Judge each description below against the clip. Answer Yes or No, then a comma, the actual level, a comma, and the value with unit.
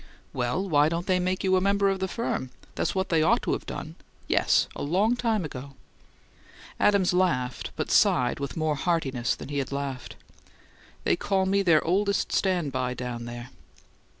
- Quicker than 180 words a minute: No, average, 175 wpm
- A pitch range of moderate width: No, wide, 6.1 semitones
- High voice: No, medium, 165 Hz